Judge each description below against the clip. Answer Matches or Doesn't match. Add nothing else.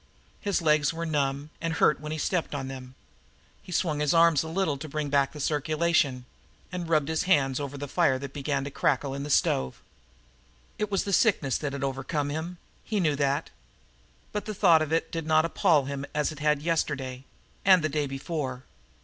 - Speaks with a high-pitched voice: Doesn't match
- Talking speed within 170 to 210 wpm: Matches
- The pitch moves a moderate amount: Matches